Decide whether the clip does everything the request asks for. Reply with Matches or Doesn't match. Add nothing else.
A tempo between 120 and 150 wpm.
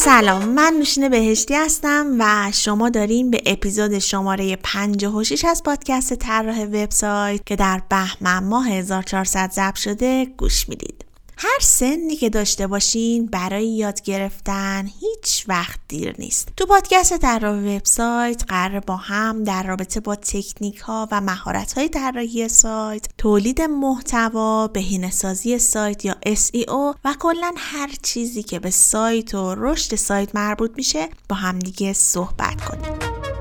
Matches